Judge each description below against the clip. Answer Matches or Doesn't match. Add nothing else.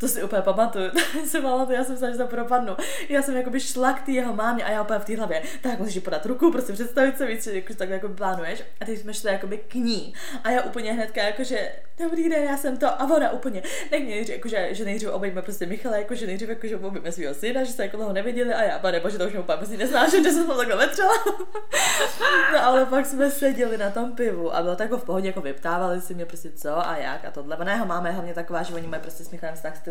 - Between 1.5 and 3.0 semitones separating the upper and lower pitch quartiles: Doesn't match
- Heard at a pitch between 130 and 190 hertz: Doesn't match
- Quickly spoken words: Matches